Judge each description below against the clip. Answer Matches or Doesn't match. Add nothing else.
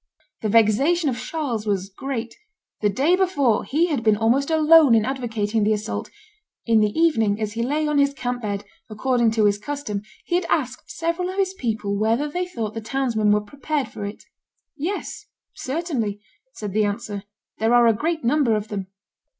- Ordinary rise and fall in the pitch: Doesn't match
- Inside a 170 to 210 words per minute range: Matches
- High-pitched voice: Matches